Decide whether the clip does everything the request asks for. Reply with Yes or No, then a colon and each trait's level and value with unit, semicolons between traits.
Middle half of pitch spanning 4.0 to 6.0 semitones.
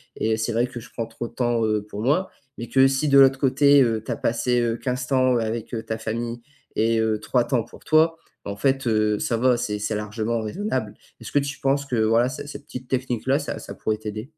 No: average, 3.2 semitones